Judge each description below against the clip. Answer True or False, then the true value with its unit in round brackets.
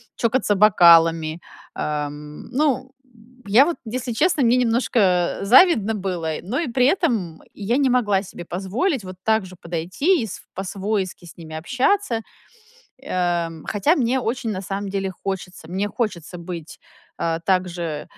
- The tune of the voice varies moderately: False (5.9 semitones)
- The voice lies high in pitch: True (195 Hz)